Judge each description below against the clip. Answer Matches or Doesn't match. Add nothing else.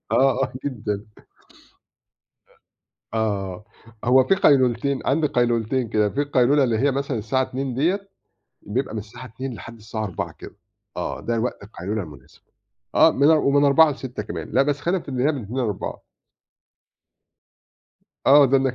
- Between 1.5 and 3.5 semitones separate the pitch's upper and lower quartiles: Doesn't match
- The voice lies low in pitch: Matches